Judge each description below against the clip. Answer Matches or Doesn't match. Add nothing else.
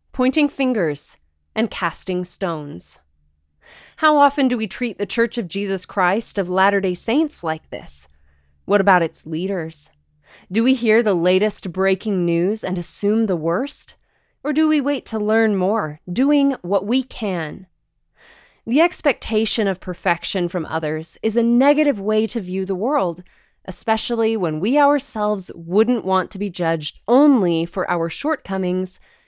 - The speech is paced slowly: Doesn't match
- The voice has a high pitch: Matches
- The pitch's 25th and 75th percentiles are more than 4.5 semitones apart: Matches